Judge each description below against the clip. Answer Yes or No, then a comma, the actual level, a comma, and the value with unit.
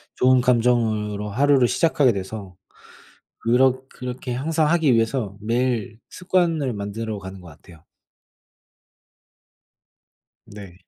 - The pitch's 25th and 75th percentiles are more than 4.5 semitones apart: No, average, 4.1 semitones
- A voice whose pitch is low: Yes, low, 120 Hz